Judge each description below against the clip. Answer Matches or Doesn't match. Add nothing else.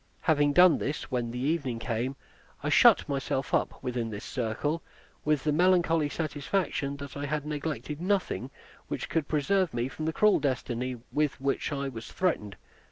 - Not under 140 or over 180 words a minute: Matches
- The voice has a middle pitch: Matches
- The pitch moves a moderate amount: Matches